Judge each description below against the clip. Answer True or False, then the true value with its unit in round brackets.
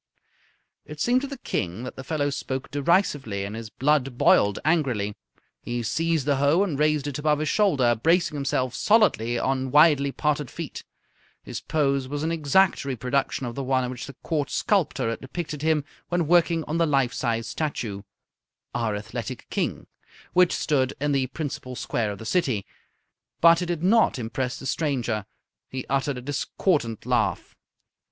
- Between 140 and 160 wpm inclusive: False (170 wpm)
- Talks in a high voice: False (140 Hz)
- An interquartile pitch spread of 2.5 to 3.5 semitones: False (4.1 semitones)